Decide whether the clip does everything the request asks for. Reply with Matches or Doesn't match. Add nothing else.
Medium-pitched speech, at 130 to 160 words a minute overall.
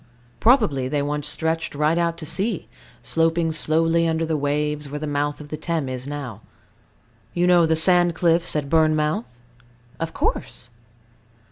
Matches